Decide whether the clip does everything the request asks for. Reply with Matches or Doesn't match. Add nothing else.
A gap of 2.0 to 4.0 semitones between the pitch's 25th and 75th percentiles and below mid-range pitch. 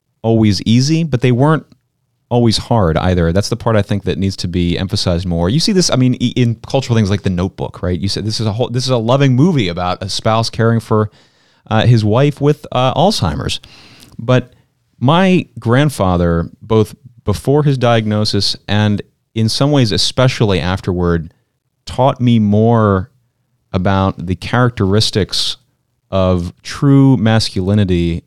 Doesn't match